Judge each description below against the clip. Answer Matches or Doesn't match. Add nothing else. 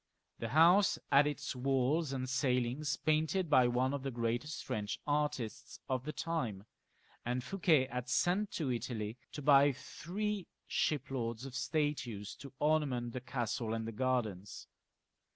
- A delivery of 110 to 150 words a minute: Matches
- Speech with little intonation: Doesn't match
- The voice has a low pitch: Matches